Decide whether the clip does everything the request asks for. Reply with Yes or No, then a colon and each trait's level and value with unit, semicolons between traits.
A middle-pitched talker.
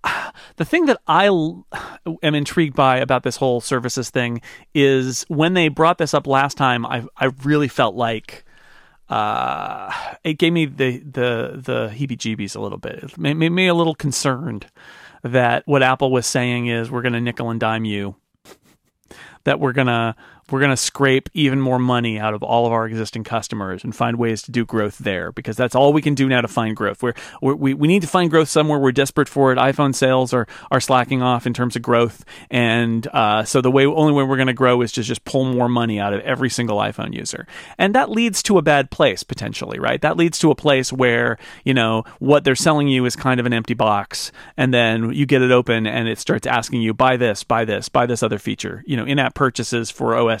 No: low, 130 Hz